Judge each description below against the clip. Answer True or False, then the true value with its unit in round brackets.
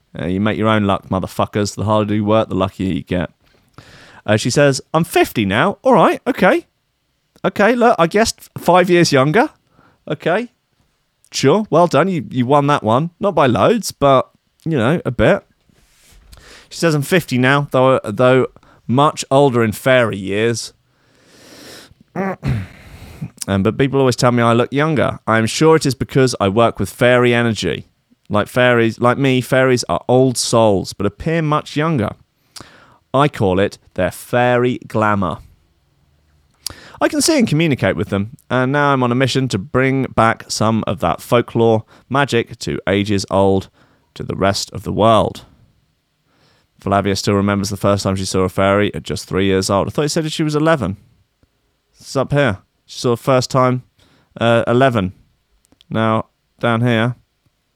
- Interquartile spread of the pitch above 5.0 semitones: True (5.4 semitones)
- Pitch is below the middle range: True (120 Hz)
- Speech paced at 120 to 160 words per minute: False (170 wpm)